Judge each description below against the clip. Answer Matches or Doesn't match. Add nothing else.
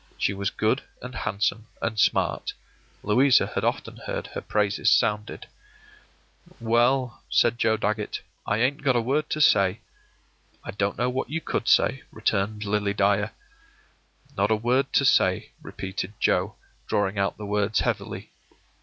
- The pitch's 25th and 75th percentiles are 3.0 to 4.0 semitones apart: Matches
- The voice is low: Matches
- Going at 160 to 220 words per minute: Doesn't match